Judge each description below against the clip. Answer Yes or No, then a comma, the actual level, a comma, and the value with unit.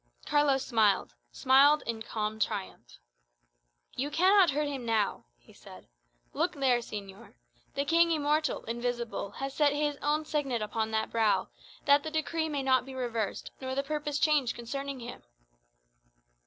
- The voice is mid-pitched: No, very high, 270 Hz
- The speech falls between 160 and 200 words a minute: No, average, 150 wpm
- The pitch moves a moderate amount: Yes, average, 4.5 semitones